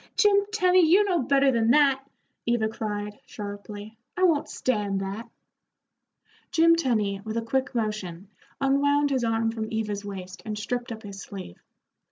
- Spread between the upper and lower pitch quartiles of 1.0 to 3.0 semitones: No, average, 5.2 semitones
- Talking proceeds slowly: No, average, 155 wpm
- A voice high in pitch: Yes, high, 225 Hz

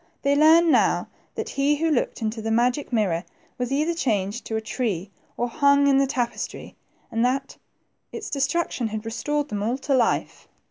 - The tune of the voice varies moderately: Yes, average, 4.2 semitones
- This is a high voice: Yes, very high, 250 Hz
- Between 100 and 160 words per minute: No, average, 180 wpm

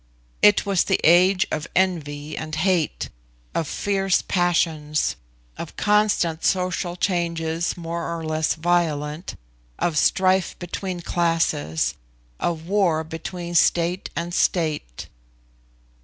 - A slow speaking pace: Yes, slow, 110 wpm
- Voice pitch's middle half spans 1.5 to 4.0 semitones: Yes, narrow, 2.5 semitones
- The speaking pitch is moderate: Yes, medium, 170 Hz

